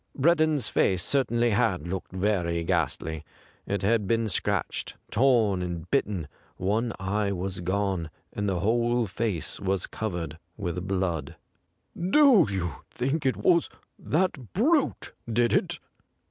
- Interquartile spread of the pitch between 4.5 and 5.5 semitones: Yes, average, 5.2 semitones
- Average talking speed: No, slow, 130 wpm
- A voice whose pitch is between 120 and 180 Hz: No, low, 100 Hz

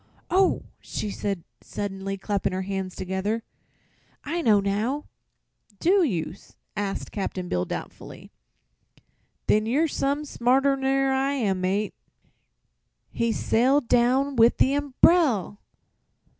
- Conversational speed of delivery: No, slow, 115 wpm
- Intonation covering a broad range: Yes, wide, 5.7 semitones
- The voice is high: Yes, high, 230 Hz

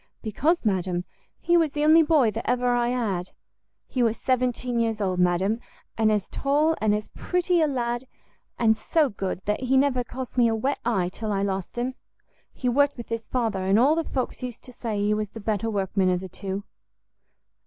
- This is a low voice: No, high, 230 Hz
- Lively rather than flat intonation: No, average, 4.2 semitones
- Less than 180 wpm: No, fast, 205 wpm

